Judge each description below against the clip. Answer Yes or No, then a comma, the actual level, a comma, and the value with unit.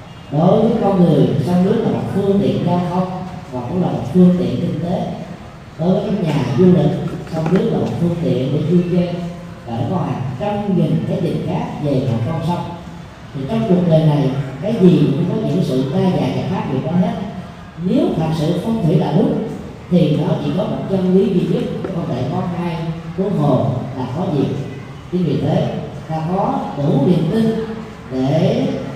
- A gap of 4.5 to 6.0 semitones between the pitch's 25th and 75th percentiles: No, average, 3.6 semitones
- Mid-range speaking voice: Yes, medium, 170 Hz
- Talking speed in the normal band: Yes, average, 205 wpm